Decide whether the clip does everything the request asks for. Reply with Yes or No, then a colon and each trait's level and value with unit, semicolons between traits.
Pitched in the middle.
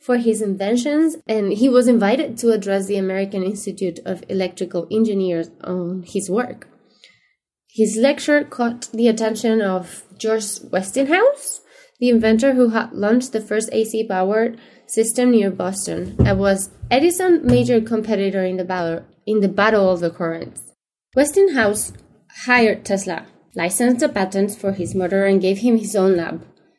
No: high, 215 Hz